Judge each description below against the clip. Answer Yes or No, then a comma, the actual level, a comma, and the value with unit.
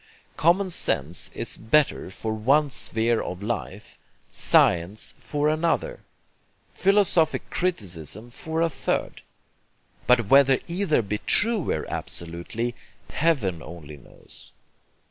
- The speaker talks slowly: Yes, slow, 105 wpm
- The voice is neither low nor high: No, low, 120 Hz